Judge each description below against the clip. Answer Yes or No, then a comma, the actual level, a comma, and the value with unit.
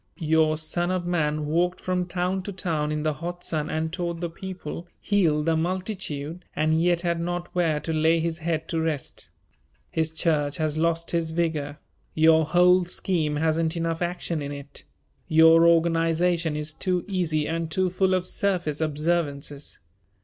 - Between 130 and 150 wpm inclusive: No, average, 165 wpm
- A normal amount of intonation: No, narrow, 2.1 semitones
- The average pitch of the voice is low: No, medium, 165 Hz